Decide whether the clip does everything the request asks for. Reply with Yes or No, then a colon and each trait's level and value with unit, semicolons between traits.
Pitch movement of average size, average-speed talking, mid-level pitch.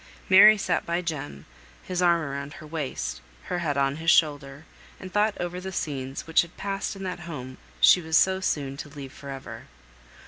Yes: average, 4.5 semitones; average, 195 wpm; medium, 160 Hz